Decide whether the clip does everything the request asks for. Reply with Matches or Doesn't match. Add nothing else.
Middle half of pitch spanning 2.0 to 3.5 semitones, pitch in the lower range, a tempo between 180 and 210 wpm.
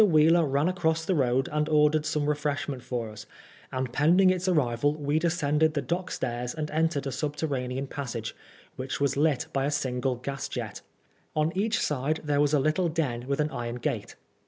Doesn't match